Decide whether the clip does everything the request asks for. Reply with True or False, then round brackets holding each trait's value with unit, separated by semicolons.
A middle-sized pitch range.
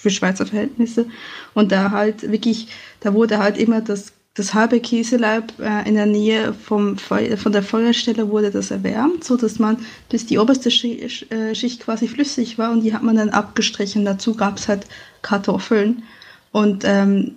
False (2.0 semitones)